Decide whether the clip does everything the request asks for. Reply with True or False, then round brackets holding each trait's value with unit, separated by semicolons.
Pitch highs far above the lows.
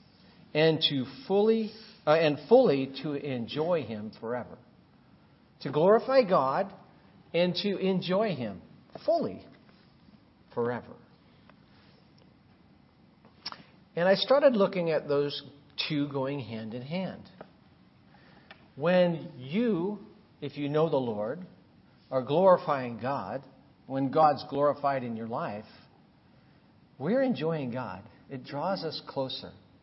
True (5.9 semitones)